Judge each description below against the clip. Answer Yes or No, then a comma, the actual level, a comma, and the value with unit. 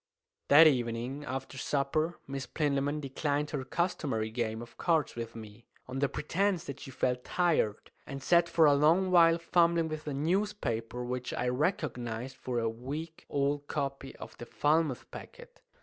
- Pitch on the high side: No, medium, 140 Hz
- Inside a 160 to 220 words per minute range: Yes, average, 165 wpm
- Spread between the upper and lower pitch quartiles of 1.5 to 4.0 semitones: No, average, 4.6 semitones